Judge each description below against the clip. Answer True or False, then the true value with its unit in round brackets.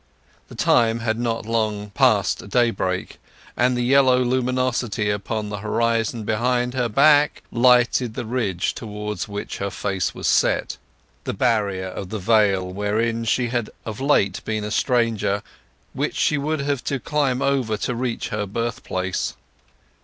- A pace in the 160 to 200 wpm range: False (145 wpm)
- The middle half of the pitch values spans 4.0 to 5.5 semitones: False (3.2 semitones)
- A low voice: True (115 Hz)